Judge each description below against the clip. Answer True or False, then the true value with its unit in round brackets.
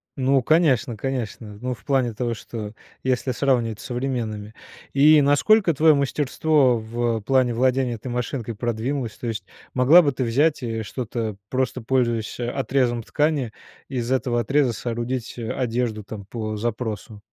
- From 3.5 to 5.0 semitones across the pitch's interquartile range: False (2.9 semitones)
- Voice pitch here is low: True (125 Hz)